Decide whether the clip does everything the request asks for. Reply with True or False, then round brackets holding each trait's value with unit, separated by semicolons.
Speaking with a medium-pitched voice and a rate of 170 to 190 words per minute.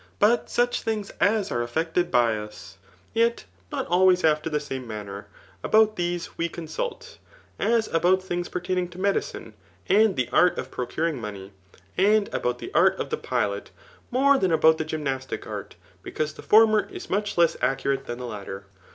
True (170 Hz; 175 wpm)